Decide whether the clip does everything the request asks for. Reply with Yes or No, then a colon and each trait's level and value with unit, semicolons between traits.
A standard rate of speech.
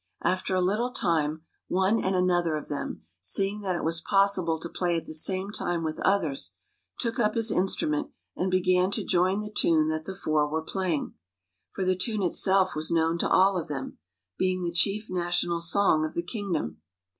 Yes: average, 190 wpm